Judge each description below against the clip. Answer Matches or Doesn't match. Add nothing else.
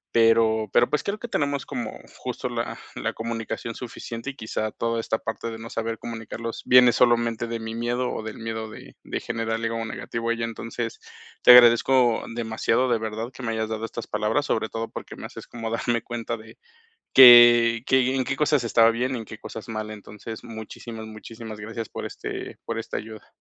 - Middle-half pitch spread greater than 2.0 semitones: Doesn't match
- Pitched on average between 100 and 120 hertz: Matches